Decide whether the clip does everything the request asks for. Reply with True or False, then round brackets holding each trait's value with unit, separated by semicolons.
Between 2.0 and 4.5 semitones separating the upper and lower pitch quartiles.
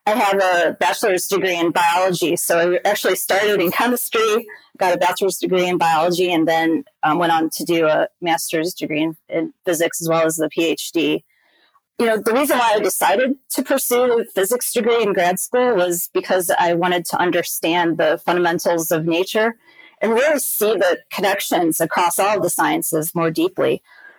False (5.6 semitones)